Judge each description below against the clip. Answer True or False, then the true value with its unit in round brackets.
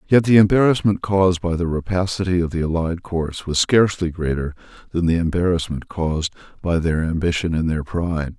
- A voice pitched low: True (85 Hz)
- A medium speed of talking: True (170 wpm)